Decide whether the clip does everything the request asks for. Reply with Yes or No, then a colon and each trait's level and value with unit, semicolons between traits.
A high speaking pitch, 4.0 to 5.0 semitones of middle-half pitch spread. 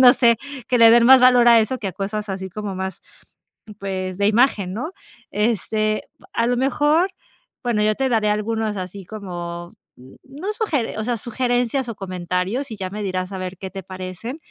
Yes: high, 215 Hz; average, 4.4 semitones